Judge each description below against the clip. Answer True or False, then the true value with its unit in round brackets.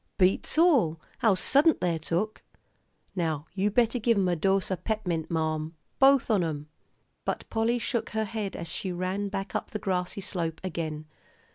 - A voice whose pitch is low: False (190 Hz)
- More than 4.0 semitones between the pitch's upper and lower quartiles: True (4.6 semitones)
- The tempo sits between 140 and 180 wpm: True (170 wpm)